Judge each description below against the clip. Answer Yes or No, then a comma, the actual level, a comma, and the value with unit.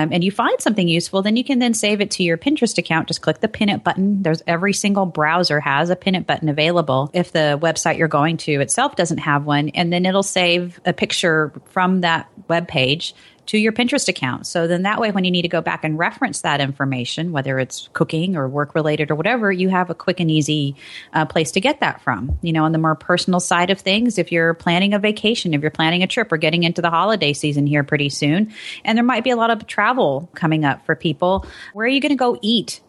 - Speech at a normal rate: No, fast, 250 wpm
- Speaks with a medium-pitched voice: Yes, medium, 175 Hz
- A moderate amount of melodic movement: Yes, average, 4.3 semitones